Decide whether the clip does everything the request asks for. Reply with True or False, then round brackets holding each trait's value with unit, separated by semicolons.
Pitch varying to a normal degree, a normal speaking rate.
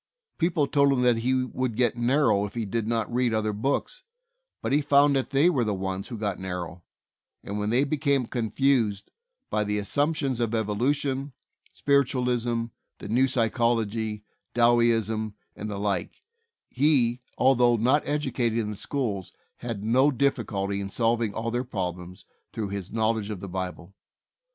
True (4.0 semitones; 165 wpm)